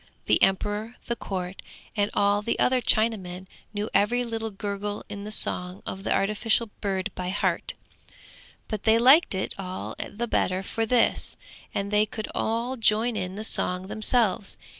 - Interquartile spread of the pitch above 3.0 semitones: No, average, 2.7 semitones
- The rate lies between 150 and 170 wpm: Yes, average, 160 wpm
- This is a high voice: Yes, high, 210 Hz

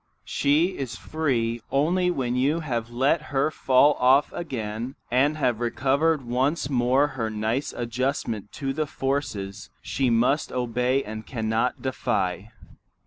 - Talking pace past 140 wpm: No, slow, 135 wpm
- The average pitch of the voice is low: Yes, low, 130 Hz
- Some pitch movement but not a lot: Yes, average, 3.5 semitones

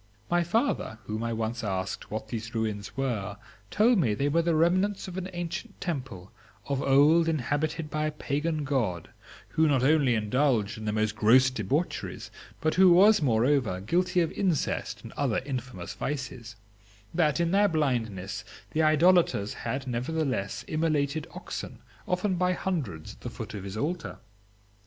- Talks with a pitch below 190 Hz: Yes, medium, 140 Hz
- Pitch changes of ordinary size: No, wide, 7.0 semitones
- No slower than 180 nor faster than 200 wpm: No, average, 160 wpm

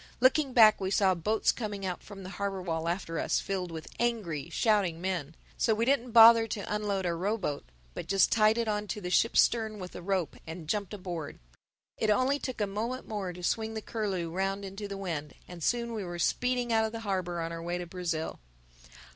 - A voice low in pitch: No, high, 195 Hz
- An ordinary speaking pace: No, fast, 215 wpm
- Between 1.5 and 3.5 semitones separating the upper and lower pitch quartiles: No, average, 3.9 semitones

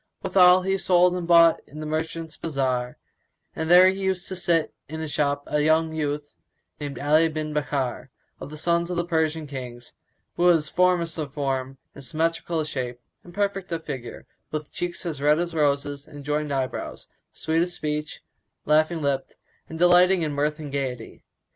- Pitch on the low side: No, medium, 155 Hz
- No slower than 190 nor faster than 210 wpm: No, average, 175 wpm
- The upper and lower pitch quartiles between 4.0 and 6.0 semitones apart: No, average, 3.1 semitones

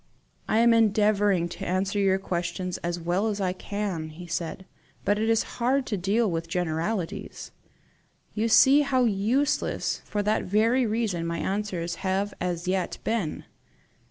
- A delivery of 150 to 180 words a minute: Yes, average, 155 wpm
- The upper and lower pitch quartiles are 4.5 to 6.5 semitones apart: No, average, 3.7 semitones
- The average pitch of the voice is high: Yes, high, 200 Hz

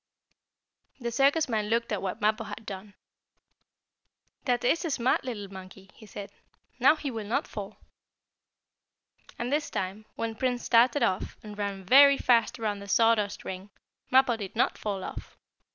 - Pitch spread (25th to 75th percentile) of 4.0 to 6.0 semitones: No, average, 3.6 semitones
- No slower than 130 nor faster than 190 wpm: Yes, average, 160 wpm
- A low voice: No, high, 220 Hz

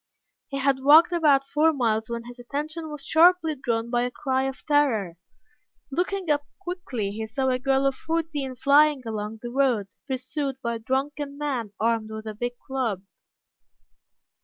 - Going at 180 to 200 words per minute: No, average, 165 wpm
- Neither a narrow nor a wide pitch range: Yes, average, 4.1 semitones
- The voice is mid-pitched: No, very high, 265 Hz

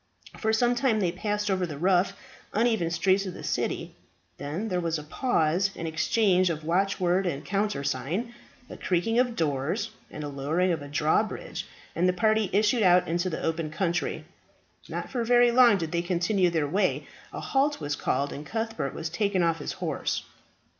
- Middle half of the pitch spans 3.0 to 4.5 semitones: No, average, 4.9 semitones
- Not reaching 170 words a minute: No, average, 180 wpm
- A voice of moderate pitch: Yes, medium, 180 Hz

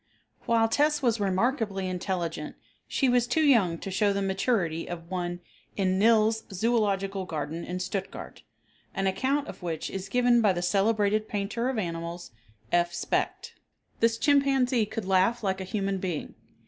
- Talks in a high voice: Yes, high, 200 Hz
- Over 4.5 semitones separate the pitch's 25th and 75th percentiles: No, average, 4.0 semitones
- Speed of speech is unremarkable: Yes, average, 155 wpm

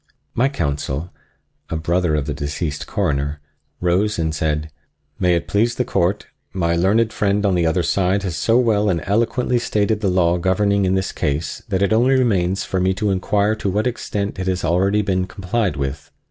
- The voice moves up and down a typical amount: Yes, average, 3.7 semitones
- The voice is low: Yes, very low, 95 Hz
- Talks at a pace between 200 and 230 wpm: No, average, 190 wpm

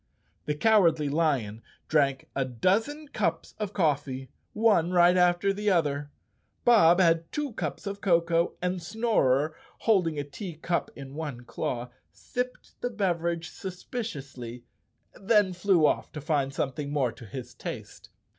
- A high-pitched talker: No, medium, 165 Hz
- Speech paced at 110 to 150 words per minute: Yes, average, 140 wpm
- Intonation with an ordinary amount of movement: No, wide, 5.7 semitones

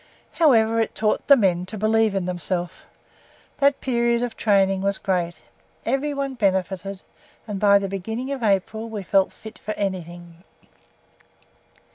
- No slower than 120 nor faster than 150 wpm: Yes, average, 140 wpm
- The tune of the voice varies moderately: Yes, average, 3.2 semitones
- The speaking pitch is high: Yes, high, 205 Hz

